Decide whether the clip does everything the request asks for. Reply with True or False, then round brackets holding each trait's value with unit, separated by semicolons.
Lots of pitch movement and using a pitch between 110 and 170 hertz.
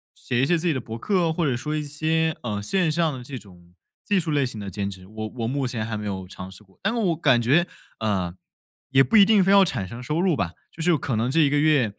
True (7.0 semitones; 135 Hz)